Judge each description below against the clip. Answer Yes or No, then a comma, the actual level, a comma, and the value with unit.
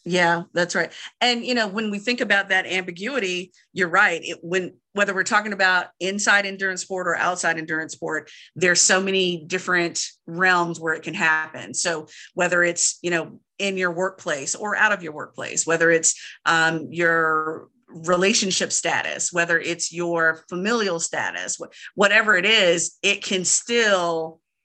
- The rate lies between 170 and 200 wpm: No, average, 160 wpm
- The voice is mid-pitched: Yes, medium, 180 Hz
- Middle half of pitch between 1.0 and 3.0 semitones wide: Yes, average, 2.7 semitones